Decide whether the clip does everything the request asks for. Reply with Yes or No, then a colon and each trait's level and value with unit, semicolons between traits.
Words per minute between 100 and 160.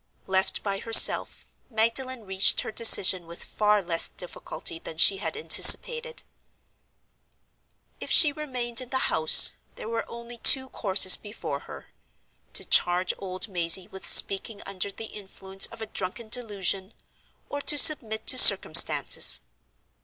Yes: slow, 135 wpm